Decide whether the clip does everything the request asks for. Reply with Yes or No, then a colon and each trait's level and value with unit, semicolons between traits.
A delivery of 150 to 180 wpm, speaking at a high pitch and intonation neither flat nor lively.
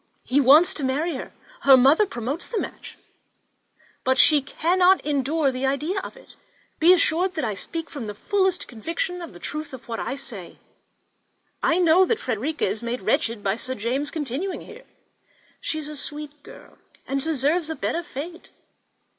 Yes: average, 175 wpm; very high, 295 Hz; average, 4.5 semitones